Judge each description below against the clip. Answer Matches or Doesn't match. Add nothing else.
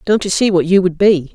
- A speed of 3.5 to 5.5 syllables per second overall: Doesn't match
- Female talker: Matches